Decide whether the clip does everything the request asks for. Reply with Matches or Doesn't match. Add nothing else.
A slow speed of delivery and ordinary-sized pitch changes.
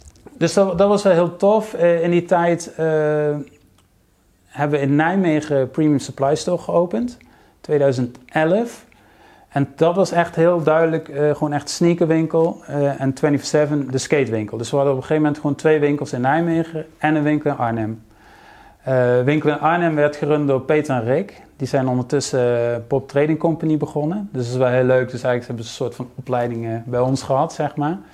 Doesn't match